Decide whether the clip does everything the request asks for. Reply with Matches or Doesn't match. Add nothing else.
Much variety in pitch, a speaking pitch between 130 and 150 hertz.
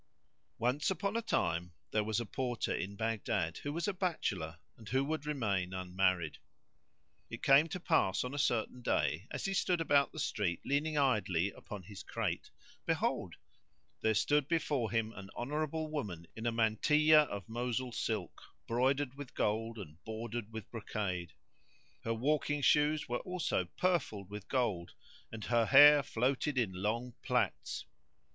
Doesn't match